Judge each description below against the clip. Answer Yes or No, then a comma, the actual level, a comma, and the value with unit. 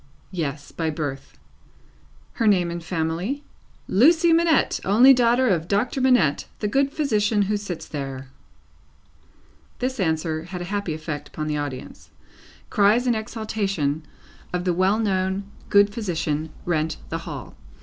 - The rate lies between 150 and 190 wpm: No, average, 140 wpm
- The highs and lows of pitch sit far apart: Yes, wide, 5.7 semitones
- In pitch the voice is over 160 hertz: Yes, high, 190 Hz